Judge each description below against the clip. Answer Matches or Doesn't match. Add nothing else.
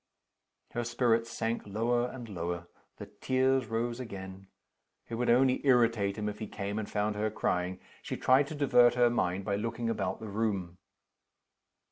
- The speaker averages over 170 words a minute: Doesn't match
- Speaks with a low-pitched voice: Matches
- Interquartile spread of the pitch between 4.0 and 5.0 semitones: Doesn't match